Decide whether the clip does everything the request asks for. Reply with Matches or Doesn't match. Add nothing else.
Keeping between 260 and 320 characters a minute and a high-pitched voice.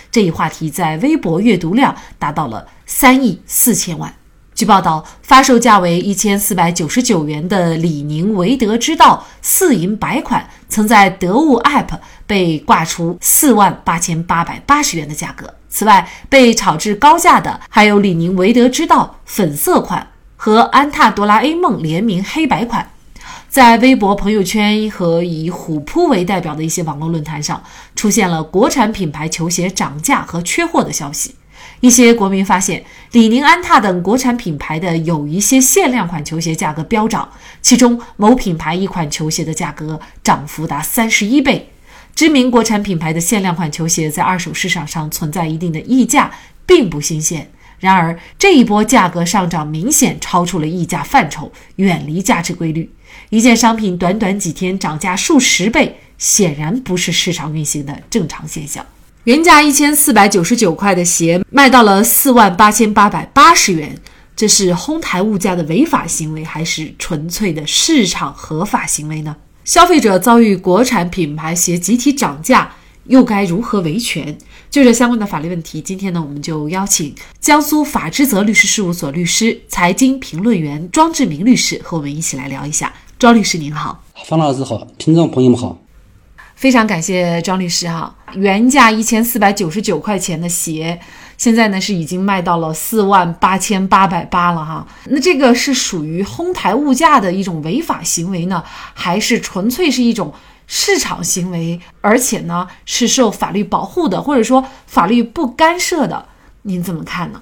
Matches